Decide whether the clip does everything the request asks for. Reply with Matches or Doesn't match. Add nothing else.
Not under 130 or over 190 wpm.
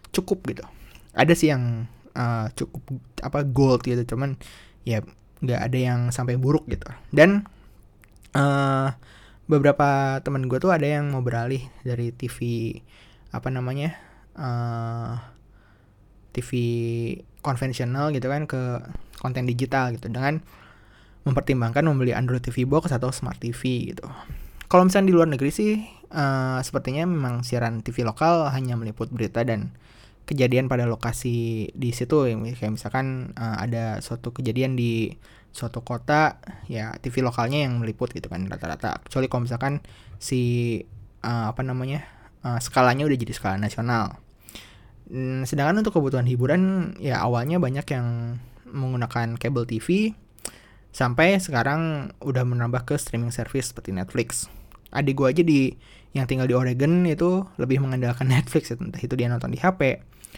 Matches